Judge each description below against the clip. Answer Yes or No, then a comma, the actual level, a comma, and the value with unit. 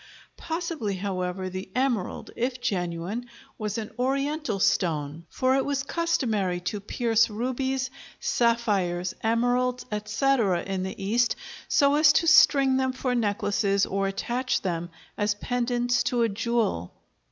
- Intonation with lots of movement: No, average, 4.7 semitones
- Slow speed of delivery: Yes, slow, 130 wpm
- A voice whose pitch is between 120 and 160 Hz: No, high, 230 Hz